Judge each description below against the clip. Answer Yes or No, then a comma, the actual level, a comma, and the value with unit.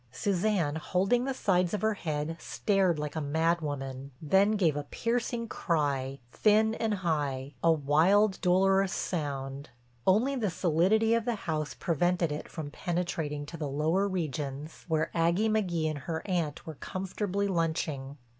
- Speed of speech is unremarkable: Yes, average, 155 wpm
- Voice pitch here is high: No, medium, 170 Hz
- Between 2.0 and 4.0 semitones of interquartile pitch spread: No, average, 4.8 semitones